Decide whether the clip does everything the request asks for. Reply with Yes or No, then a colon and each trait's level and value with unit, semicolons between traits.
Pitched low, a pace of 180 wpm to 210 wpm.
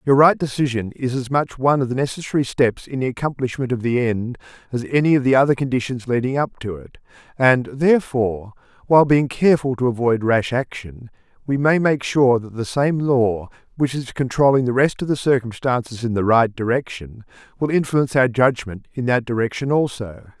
Yes: low, 125 Hz; average, 190 wpm